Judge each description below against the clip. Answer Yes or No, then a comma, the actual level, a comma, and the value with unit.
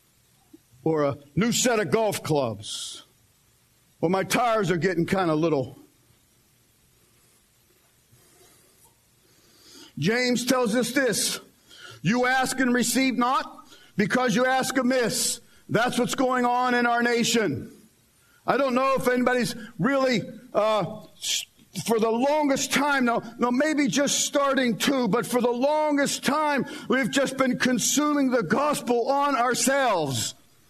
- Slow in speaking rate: Yes, slow, 125 wpm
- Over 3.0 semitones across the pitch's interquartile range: Yes, average, 3.6 semitones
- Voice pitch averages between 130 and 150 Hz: No, high, 245 Hz